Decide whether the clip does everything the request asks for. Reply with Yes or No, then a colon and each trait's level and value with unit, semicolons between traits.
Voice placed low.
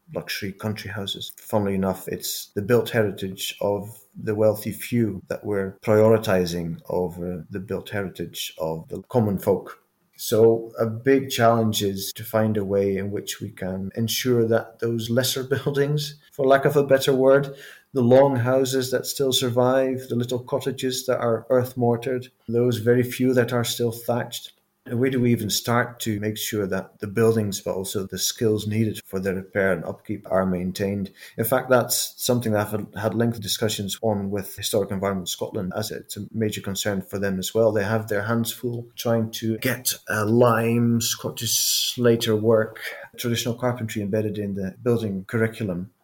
Yes: low, 110 Hz